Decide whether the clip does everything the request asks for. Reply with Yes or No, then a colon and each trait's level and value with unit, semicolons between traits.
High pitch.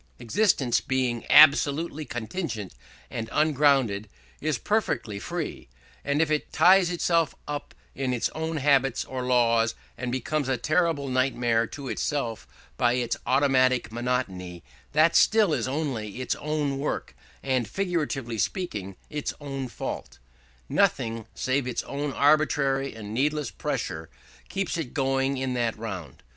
No: low, 135 Hz